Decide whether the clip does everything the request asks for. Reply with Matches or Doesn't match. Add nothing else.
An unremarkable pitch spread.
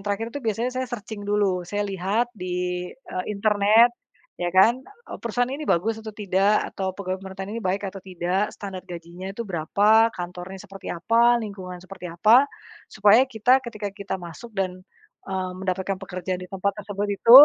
Matches